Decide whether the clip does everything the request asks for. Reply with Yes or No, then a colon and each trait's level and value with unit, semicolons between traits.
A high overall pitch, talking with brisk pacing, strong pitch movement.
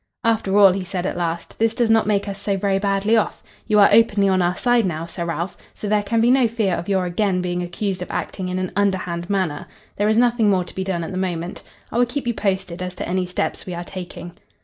No: high, 195 Hz; fast, 260 wpm; average, 2.8 semitones